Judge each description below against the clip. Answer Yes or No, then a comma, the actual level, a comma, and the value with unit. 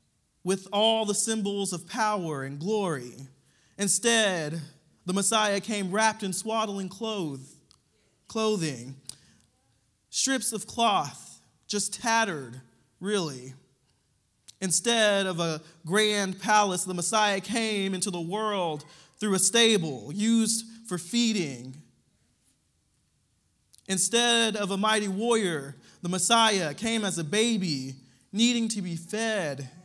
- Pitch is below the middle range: No, high, 195 Hz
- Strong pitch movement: Yes, wide, 6.1 semitones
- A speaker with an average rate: No, slow, 110 wpm